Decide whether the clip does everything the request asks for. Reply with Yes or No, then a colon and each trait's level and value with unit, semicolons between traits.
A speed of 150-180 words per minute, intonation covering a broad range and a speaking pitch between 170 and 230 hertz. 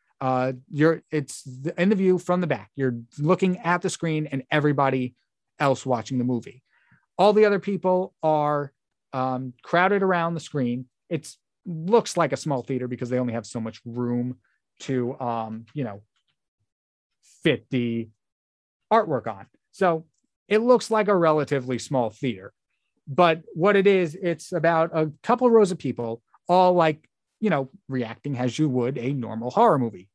No: average, 165 wpm; wide, 5.8 semitones; medium, 140 Hz